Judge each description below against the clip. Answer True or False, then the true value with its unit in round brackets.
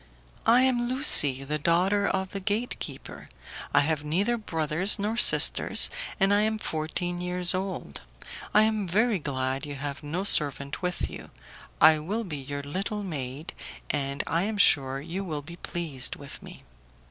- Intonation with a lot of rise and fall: True (5.8 semitones)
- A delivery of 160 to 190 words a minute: True (165 wpm)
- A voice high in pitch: False (175 Hz)